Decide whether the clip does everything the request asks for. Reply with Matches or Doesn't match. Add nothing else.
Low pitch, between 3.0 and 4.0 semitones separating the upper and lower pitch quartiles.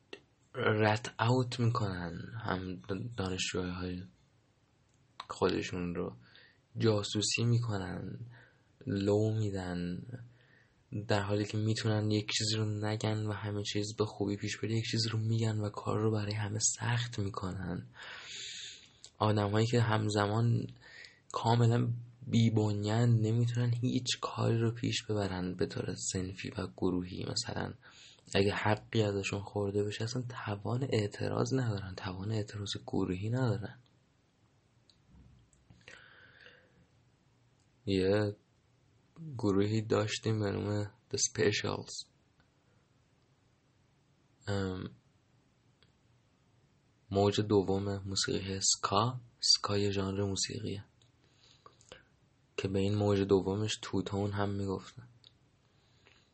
Matches